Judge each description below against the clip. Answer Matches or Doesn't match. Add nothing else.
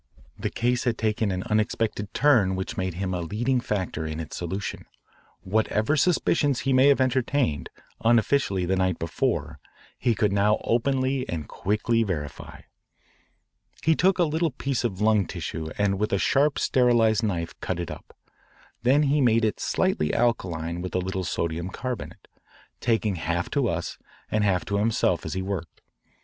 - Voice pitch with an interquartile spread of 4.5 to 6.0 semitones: Matches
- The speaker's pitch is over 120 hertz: Doesn't match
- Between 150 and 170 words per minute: Matches